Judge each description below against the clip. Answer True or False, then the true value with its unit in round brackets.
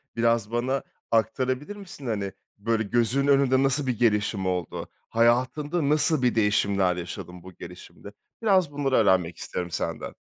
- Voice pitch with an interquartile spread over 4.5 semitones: True (5.3 semitones)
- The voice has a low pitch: True (115 Hz)